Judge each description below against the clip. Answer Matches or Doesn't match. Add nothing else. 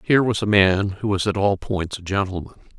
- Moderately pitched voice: Doesn't match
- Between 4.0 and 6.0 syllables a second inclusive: Matches